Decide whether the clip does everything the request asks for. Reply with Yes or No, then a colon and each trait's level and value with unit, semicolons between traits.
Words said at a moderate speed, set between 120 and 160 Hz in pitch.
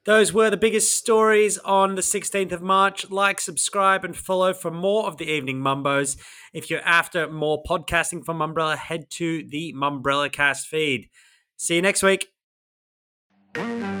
No: average, 165 wpm; medium, 175 Hz